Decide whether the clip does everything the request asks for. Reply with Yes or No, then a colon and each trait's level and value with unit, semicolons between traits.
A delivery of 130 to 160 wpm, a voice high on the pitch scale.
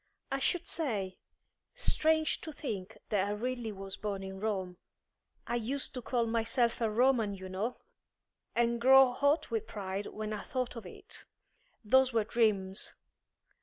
Yes: average, 155 wpm; high, 230 Hz